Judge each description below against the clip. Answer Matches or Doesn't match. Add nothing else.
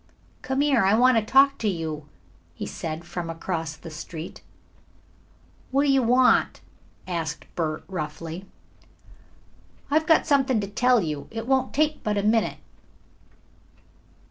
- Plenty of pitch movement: Matches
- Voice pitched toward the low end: Doesn't match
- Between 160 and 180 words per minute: Doesn't match